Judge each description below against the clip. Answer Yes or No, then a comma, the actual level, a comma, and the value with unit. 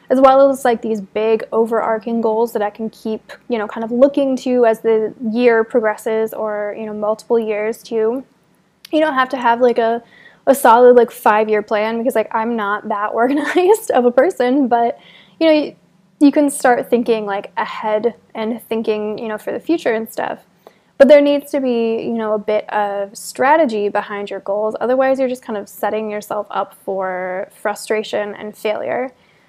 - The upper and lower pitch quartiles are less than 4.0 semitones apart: Yes, average, 3.0 semitones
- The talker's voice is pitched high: Yes, high, 225 Hz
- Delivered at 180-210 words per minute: Yes, average, 195 wpm